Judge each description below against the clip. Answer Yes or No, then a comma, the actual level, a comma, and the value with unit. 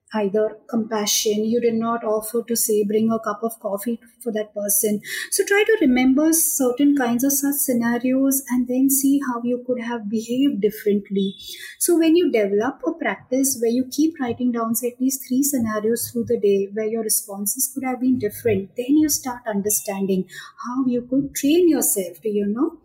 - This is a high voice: Yes, high, 235 Hz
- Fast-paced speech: No, average, 190 wpm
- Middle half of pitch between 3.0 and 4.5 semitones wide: Yes, average, 3.8 semitones